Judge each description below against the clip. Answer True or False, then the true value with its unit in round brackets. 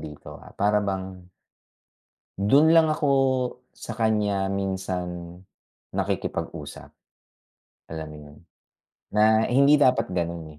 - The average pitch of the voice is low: True (100 Hz)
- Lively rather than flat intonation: False (4.3 semitones)